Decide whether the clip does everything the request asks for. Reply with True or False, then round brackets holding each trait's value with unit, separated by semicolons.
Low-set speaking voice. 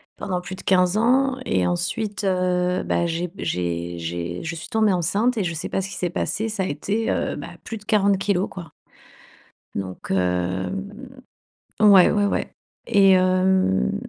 False (185 Hz)